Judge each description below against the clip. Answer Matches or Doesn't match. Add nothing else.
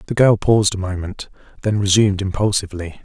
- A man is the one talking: Matches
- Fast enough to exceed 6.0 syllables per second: Matches